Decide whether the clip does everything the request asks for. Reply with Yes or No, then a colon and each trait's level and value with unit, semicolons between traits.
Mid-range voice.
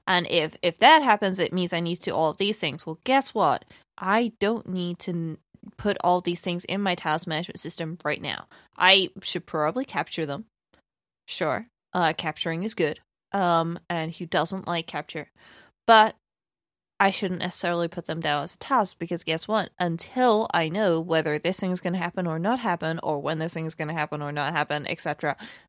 Yes: medium, 175 Hz